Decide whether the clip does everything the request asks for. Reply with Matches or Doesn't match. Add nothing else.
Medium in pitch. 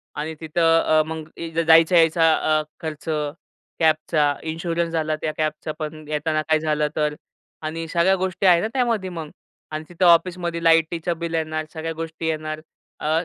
Matches